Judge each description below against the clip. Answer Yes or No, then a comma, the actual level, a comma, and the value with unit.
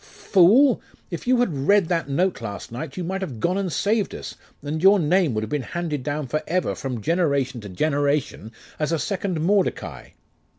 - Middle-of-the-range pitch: Yes, medium, 160 Hz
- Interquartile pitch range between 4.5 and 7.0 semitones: Yes, average, 5.1 semitones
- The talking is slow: No, average, 195 wpm